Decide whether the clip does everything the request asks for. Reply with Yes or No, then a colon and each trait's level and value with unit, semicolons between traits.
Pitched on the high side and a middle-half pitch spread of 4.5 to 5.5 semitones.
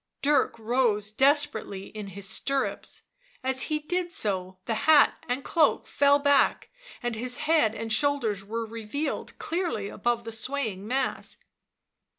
Yes: high, 245 Hz; average, 4.9 semitones